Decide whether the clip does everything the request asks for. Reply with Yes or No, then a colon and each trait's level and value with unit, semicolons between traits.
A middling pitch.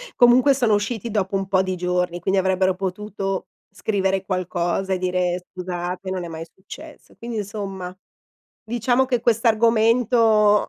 No: high, 195 Hz